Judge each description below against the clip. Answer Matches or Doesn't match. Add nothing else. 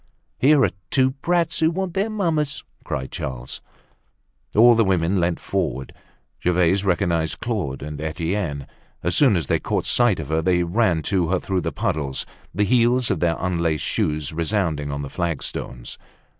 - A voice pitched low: Matches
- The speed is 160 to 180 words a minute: Matches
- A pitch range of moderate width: Doesn't match